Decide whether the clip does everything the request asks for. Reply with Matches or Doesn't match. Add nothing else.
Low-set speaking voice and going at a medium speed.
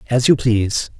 Matches